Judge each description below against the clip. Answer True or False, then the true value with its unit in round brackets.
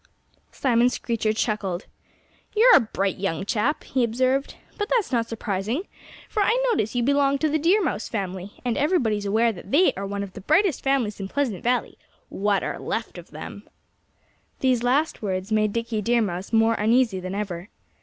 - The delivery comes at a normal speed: True (185 wpm)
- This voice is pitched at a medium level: False (230 Hz)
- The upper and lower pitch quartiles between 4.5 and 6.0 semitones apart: True (5.1 semitones)